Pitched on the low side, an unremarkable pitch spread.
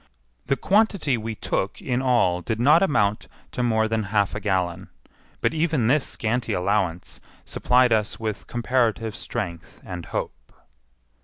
Yes: low, 110 Hz; average, 4.0 semitones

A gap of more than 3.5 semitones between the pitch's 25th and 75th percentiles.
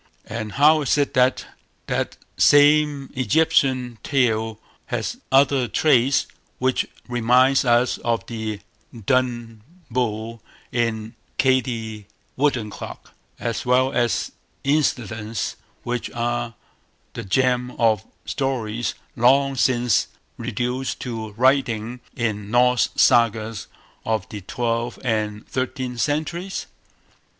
No: average, 2.7 semitones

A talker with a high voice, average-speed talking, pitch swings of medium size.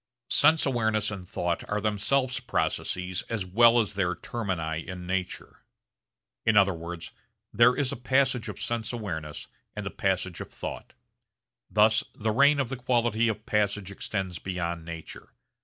No: low, 105 Hz; average, 155 wpm; average, 4.5 semitones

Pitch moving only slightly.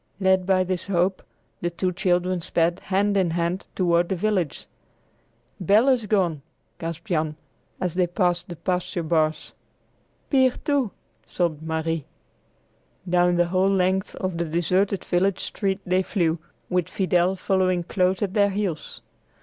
Yes: narrow, 1.9 semitones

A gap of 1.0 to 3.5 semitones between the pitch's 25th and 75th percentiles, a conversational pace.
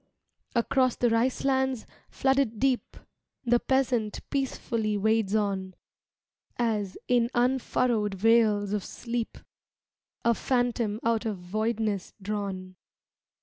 No: average, 2.9 semitones; slow, 105 wpm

